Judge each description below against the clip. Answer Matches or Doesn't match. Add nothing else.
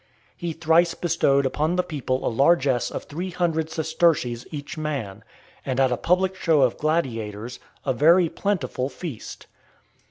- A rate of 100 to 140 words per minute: Doesn't match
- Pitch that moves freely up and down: Doesn't match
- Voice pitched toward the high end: Doesn't match